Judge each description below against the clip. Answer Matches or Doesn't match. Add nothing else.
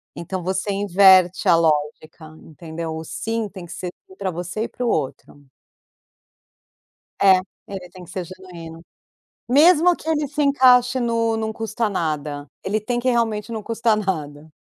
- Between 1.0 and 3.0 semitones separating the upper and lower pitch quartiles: Doesn't match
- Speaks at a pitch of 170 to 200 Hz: Matches